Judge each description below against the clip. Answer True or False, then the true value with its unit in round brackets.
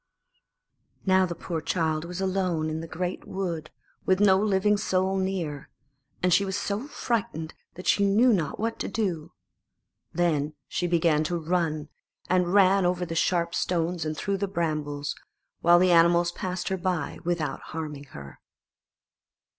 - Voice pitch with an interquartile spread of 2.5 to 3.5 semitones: True (3.0 semitones)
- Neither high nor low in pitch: True (175 Hz)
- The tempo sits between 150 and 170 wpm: True (155 wpm)